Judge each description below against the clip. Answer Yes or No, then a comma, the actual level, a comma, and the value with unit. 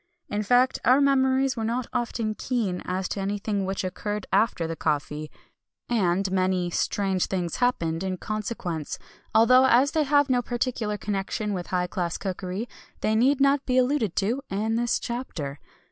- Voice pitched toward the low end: No, high, 210 Hz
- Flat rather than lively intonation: No, average, 5.1 semitones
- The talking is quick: No, average, 160 wpm